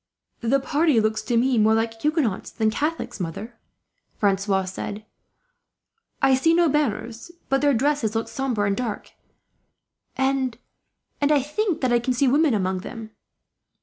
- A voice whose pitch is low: No, high, 240 Hz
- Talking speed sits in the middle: Yes, average, 150 wpm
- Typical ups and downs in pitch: Yes, average, 4.5 semitones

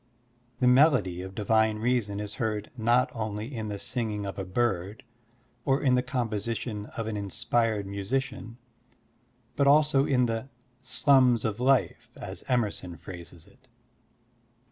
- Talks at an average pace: Yes, average, 150 wpm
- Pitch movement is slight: No, average, 3.5 semitones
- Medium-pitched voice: No, low, 115 Hz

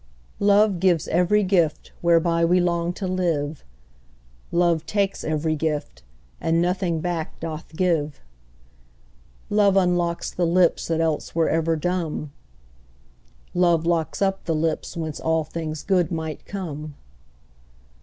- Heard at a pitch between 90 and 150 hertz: No, medium, 170 Hz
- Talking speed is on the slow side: Yes, slow, 125 wpm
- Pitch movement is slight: Yes, narrow, 2.1 semitones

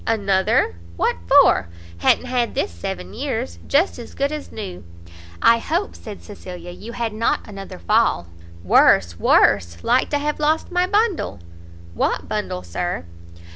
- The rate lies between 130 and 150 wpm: Yes, average, 145 wpm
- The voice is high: Yes, high, 210 Hz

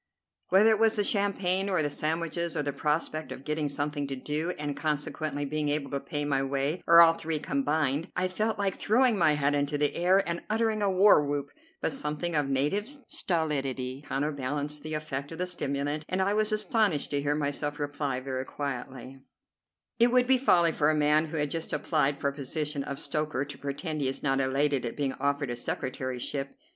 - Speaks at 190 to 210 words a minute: Yes, average, 200 wpm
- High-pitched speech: No, medium, 150 Hz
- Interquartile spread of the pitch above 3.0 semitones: Yes, average, 3.4 semitones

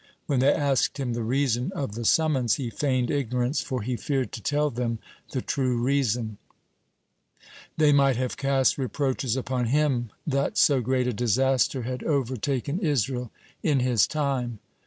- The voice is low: Yes, low, 130 Hz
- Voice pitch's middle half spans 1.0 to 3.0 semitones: Yes, narrow, 2.5 semitones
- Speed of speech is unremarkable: Yes, average, 155 wpm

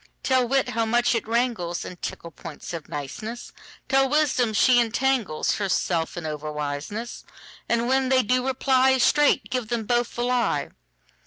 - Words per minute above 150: No, slow, 135 wpm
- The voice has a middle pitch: No, high, 235 Hz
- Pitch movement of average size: No, wide, 6.5 semitones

